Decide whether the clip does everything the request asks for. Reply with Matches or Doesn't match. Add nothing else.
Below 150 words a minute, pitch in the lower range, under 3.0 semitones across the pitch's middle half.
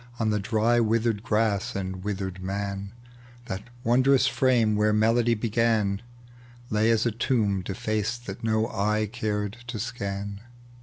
Matches